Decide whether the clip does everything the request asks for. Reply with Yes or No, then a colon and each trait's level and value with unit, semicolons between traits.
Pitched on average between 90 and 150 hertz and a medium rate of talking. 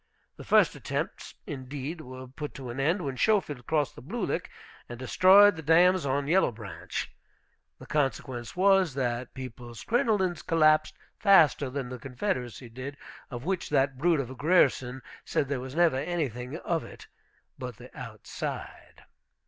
Yes: medium, 140 Hz; average, 155 wpm